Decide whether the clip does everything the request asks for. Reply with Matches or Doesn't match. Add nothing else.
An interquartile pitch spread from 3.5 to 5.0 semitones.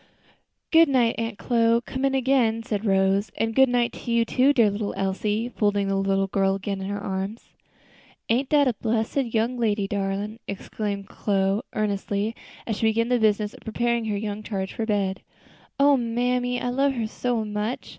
Doesn't match